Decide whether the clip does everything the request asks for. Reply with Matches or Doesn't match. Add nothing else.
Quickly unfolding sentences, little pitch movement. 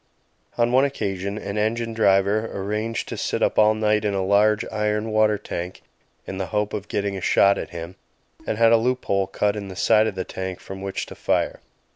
Matches